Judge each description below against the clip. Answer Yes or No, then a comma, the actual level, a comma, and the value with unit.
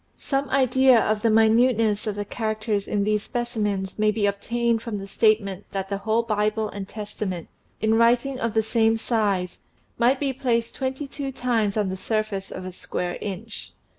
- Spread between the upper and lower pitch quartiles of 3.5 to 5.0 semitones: No, narrow, 2.6 semitones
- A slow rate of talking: No, average, 180 wpm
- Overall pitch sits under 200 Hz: No, high, 220 Hz